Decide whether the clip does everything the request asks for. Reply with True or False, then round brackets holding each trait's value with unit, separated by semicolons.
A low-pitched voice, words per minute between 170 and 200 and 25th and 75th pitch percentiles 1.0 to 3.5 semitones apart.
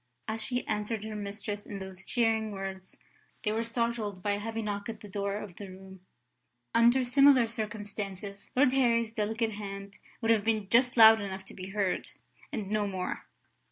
False (210 Hz; 180 wpm; 2.4 semitones)